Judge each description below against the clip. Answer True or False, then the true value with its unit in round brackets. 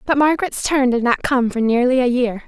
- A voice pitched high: True (255 Hz)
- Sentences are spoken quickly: True (240 wpm)